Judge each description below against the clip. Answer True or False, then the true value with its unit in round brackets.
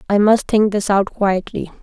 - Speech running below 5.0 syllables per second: True (4.6 syllables/s)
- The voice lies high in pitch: True (205 Hz)